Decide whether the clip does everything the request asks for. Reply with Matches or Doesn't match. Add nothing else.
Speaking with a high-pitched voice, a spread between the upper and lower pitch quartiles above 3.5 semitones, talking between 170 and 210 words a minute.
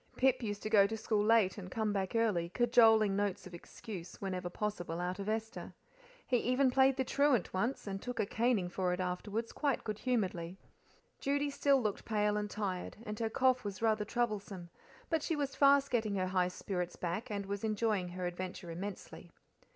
Matches